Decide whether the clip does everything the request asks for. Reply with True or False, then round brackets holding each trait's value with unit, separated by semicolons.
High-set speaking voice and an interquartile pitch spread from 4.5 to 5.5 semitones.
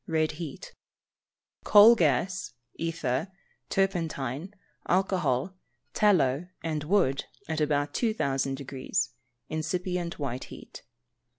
False (160 Hz; 5.0 semitones)